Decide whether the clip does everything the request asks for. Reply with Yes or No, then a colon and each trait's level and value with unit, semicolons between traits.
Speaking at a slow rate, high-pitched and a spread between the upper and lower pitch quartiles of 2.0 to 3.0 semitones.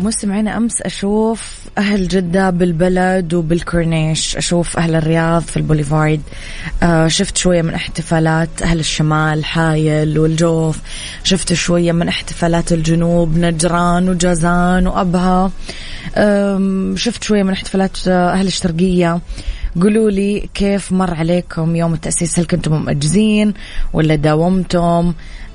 No: slow, 110 wpm; medium, 175 Hz; narrow, 2.5 semitones